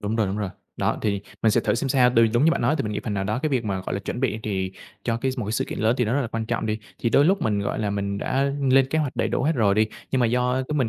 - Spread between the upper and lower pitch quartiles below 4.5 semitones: Yes, average, 4.1 semitones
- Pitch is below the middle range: Yes, low, 115 Hz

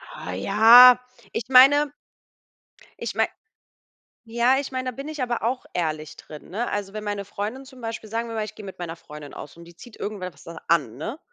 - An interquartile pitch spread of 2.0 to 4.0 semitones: No, wide, 6.2 semitones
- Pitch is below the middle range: No, high, 215 Hz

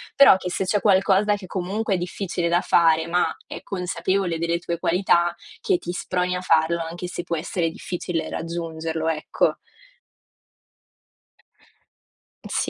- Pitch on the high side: No, medium, 175 Hz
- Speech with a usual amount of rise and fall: No, narrow, 2.1 semitones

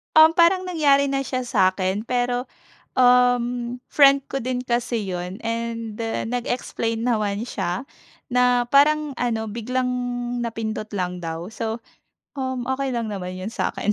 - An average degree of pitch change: Yes, average, 3.1 semitones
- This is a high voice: Yes, high, 240 Hz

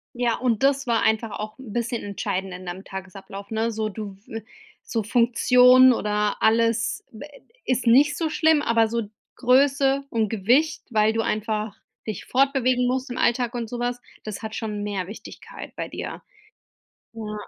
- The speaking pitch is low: No, high, 230 Hz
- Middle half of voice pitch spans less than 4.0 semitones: Yes, average, 2.9 semitones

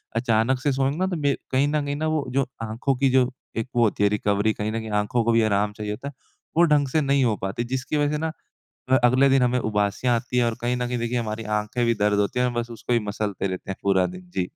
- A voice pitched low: Yes, low, 120 Hz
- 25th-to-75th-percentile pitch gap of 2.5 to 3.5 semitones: No, average, 4.3 semitones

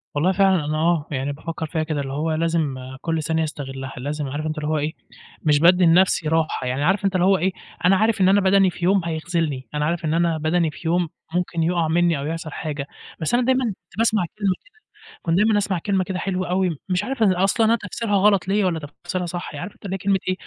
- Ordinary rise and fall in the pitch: Yes, average, 3.4 semitones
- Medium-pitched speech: Yes, medium, 170 Hz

